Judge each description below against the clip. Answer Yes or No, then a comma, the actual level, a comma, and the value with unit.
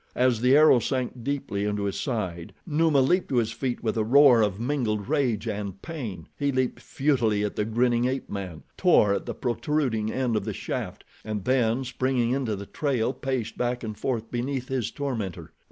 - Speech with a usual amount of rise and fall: Yes, average, 3.7 semitones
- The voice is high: No, low, 120 Hz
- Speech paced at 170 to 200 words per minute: Yes, average, 190 wpm